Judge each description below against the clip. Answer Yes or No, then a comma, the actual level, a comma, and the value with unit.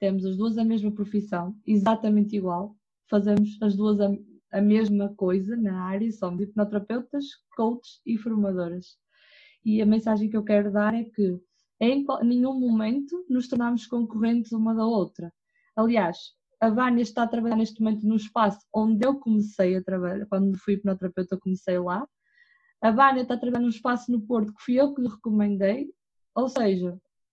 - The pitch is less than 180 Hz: No, high, 220 Hz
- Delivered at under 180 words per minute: Yes, average, 170 wpm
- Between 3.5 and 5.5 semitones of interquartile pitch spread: No, average, 3.0 semitones